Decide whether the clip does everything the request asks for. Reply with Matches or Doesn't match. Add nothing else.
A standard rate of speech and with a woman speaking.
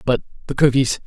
Doesn't match